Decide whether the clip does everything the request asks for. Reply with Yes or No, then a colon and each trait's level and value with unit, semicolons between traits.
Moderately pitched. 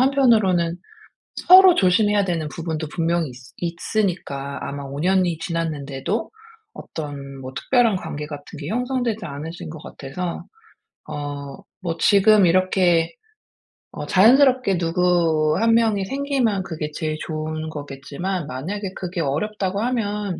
Yes: medium, 175 Hz